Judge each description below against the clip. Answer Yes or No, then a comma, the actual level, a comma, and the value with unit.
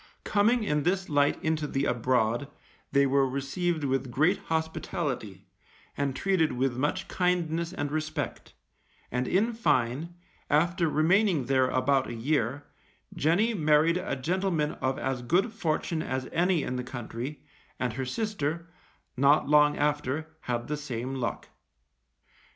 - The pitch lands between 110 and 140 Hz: No, medium, 150 Hz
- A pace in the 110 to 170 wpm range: Yes, average, 140 wpm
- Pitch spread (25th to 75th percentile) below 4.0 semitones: No, average, 4.5 semitones